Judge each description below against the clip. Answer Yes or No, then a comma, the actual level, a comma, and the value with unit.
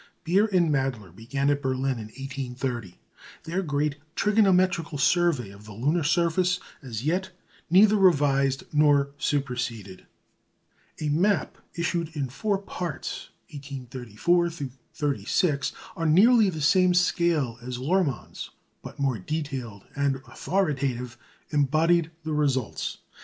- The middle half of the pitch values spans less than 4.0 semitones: No, average, 4.8 semitones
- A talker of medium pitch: Yes, medium, 145 Hz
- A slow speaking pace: Yes, slow, 115 wpm